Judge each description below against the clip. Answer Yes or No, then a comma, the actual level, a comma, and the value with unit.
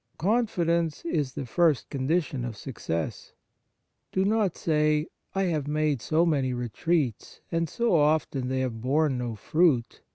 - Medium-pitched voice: Yes, medium, 150 Hz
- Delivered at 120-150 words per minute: Yes, average, 140 wpm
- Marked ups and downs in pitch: No, average, 4.6 semitones